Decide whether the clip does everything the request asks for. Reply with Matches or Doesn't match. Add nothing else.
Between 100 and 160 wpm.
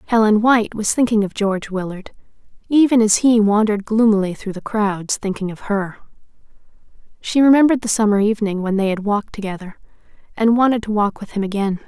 Doesn't match